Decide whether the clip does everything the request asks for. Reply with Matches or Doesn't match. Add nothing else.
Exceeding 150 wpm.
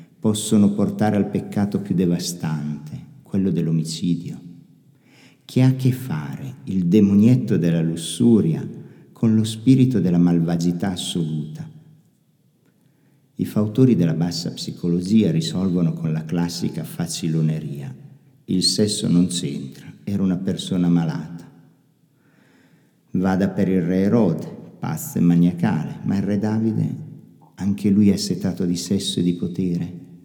Doesn't match